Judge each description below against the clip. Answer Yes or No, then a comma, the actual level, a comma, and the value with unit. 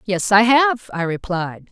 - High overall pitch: Yes, high, 210 Hz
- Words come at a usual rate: Yes, average, 175 wpm